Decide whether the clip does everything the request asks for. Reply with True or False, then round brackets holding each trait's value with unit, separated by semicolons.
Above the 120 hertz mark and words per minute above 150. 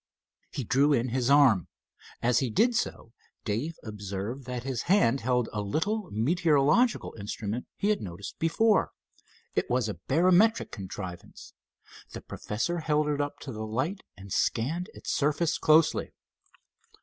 False (135 Hz; 145 wpm)